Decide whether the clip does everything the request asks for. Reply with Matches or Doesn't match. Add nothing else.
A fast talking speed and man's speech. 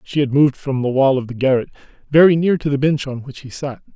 Matches